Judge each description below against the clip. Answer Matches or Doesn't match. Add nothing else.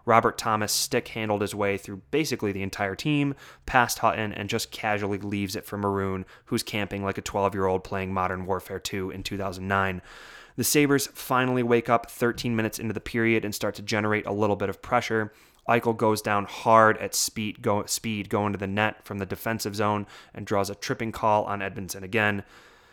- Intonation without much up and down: Matches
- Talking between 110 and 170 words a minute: Doesn't match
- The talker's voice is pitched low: Matches